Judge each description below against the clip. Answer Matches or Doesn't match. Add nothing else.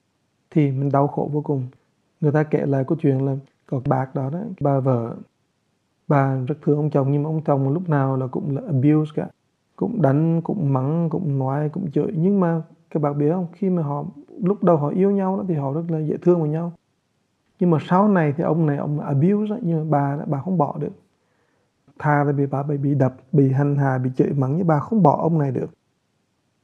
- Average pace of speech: Doesn't match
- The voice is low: Doesn't match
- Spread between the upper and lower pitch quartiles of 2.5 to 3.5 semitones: Matches